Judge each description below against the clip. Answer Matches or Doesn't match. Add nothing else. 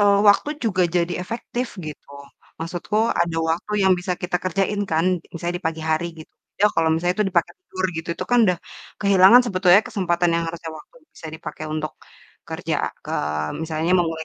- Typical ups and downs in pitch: Matches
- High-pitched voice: Doesn't match